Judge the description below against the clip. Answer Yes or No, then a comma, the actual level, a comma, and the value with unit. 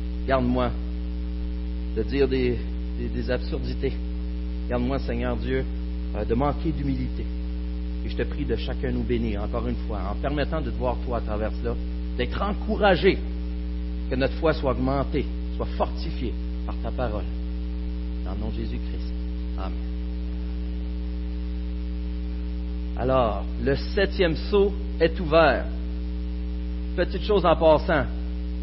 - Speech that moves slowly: Yes, slow, 130 wpm